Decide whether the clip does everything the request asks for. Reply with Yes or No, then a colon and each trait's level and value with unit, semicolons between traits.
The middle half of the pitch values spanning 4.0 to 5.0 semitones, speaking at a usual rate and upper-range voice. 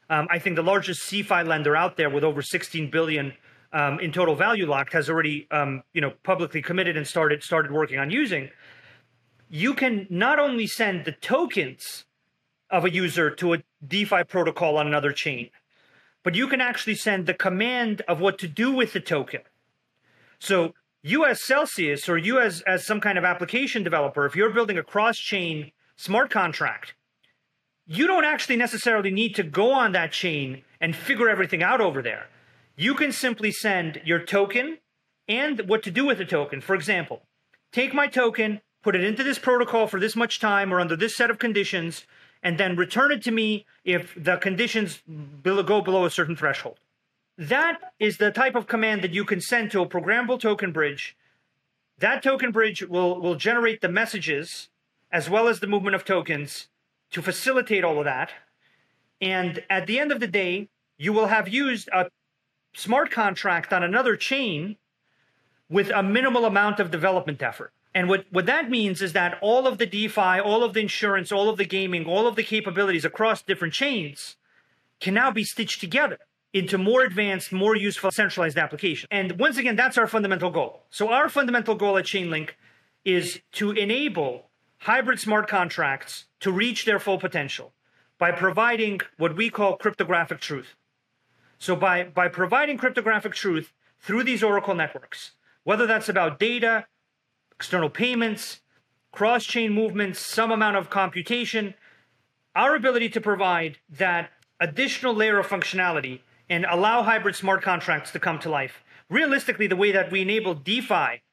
Yes: average, 4.5 semitones; average, 175 wpm; high, 195 Hz